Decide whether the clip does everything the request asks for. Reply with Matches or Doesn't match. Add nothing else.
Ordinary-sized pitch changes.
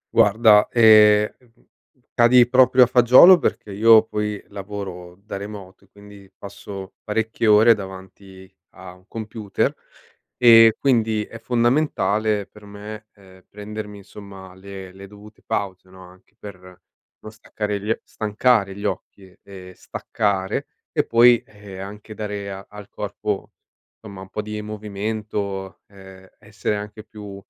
Doesn't match